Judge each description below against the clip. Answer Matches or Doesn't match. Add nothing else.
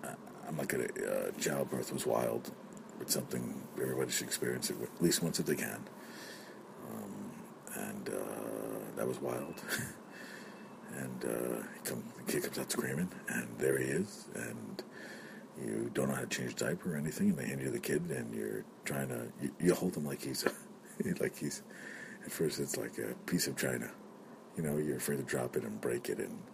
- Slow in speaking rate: Doesn't match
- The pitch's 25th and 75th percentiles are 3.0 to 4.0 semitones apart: Matches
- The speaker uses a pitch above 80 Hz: Doesn't match